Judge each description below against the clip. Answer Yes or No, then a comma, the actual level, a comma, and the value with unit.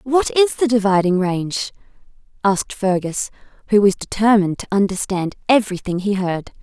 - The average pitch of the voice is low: No, high, 205 Hz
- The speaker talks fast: No, slow, 135 wpm